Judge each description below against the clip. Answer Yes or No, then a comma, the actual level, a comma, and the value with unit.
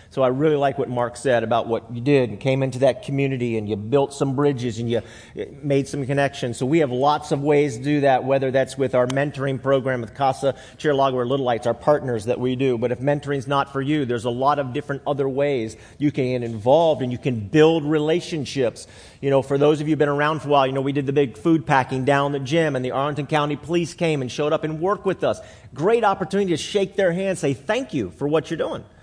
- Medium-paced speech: No, fast, 255 wpm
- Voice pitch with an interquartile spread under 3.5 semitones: Yes, average, 2.8 semitones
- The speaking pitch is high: No, medium, 140 Hz